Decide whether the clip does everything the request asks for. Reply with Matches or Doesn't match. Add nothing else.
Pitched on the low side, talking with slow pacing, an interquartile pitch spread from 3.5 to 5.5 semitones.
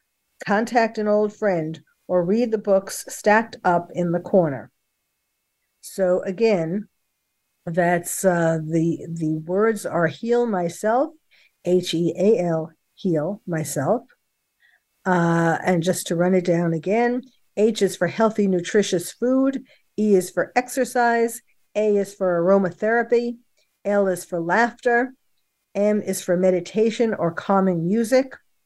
Doesn't match